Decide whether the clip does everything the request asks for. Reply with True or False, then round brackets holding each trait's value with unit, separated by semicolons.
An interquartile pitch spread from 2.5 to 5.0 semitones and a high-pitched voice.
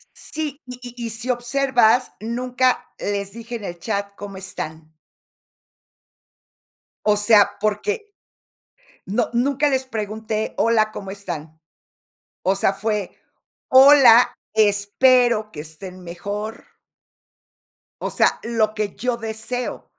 True (3.5 semitones; 220 Hz)